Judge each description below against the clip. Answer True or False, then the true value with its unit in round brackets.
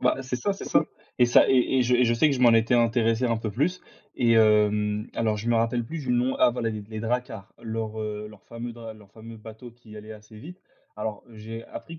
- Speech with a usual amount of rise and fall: False (2.2 semitones)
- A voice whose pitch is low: True (115 Hz)